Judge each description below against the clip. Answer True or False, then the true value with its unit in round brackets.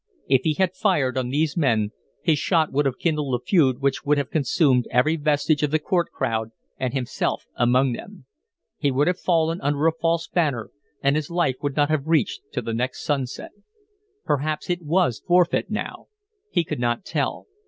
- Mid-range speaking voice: True (145 Hz)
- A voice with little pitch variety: False (3.9 semitones)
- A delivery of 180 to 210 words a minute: True (190 wpm)